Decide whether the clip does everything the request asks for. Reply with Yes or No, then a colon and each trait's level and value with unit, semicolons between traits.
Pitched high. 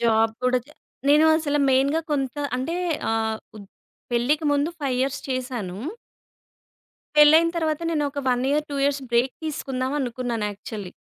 Yes: very high, 265 Hz